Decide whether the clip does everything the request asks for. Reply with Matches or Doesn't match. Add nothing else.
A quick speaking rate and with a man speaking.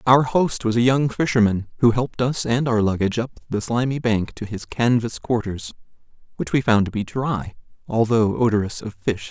Doesn't match